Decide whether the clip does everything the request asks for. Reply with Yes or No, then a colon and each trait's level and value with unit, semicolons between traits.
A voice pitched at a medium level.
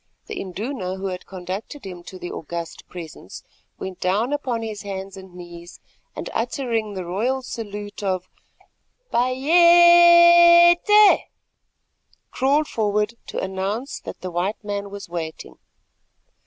No: high, 205 Hz